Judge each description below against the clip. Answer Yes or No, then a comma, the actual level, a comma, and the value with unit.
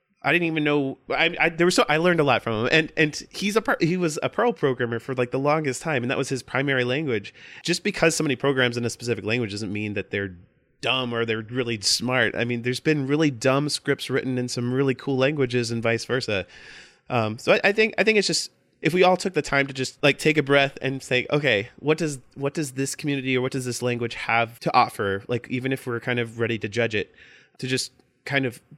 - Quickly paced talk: Yes, fast, 250 wpm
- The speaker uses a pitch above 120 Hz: Yes, low, 130 Hz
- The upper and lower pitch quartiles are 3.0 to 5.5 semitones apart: Yes, average, 3.9 semitones